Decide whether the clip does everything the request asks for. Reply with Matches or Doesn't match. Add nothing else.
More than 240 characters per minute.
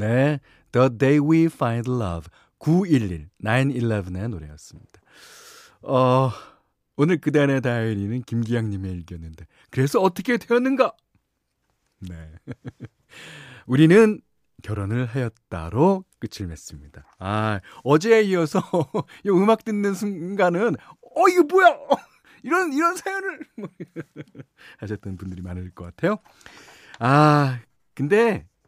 Doesn't match